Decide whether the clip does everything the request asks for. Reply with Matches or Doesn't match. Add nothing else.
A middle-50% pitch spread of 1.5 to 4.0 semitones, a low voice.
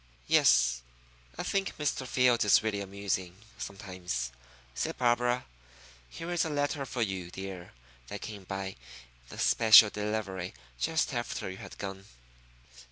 Doesn't match